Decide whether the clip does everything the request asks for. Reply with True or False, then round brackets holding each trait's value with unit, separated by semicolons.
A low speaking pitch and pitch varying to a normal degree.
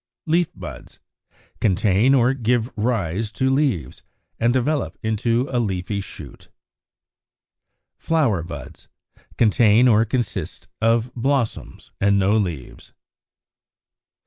True (115 Hz; 4.0 semitones)